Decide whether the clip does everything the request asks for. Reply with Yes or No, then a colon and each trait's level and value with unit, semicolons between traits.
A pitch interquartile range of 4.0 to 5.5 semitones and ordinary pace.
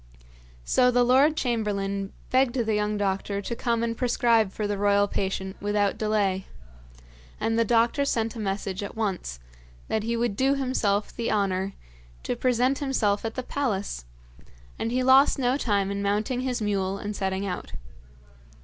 No: average, 3.6 semitones; average, 165 wpm